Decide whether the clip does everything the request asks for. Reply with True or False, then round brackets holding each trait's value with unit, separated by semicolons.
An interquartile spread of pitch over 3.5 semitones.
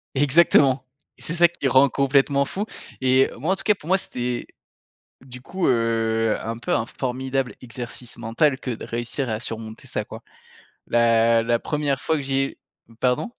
False (3.2 semitones)